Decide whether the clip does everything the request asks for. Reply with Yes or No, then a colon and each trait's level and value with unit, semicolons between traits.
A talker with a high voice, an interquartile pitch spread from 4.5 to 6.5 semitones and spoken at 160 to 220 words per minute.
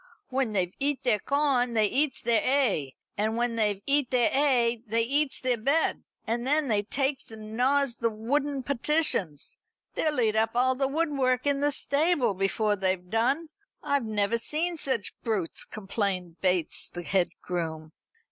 Yes: high, 235 Hz; average, 5.0 semitones; average, 165 wpm